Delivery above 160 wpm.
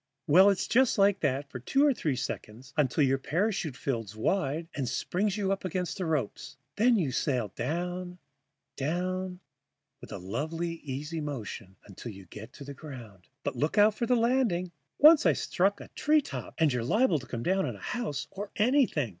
Yes: average, 190 wpm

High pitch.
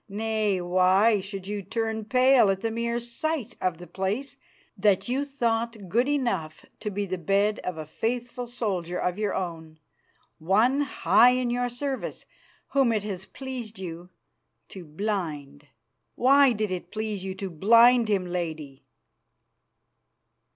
Yes: high, 210 Hz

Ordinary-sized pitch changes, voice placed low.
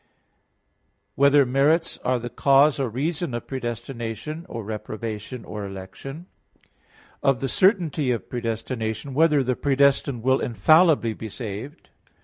Yes: average, 4.1 semitones; low, 130 Hz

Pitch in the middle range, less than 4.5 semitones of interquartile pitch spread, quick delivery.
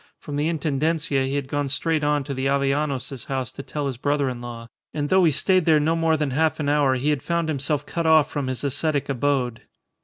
Yes: medium, 145 Hz; narrow, 2.5 semitones; fast, 235 wpm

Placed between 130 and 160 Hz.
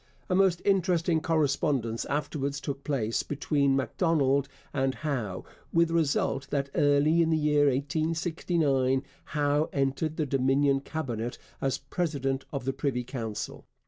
Yes: medium, 140 Hz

